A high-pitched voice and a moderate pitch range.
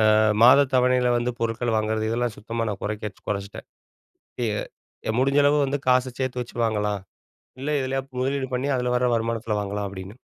No: low, 120 Hz; average, 3.1 semitones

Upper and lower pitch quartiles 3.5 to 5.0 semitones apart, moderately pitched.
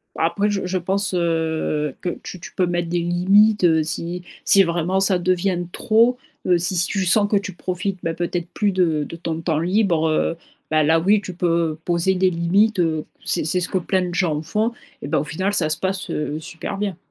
No: average, 2.8 semitones; medium, 175 Hz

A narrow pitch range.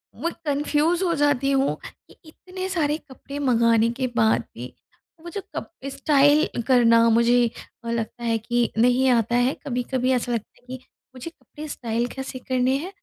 No: average, 3.6 semitones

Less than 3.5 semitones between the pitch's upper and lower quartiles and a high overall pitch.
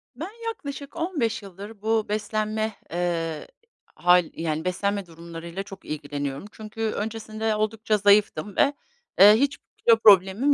No: average, 4.0 semitones; high, 210 Hz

